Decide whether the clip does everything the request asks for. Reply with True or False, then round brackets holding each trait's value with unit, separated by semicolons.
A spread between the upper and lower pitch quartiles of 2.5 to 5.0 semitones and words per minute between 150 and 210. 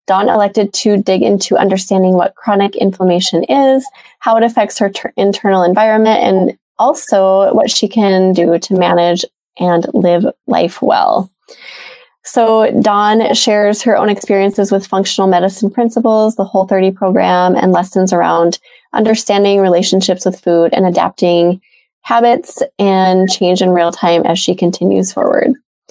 False (3.1 semitones; 140 wpm)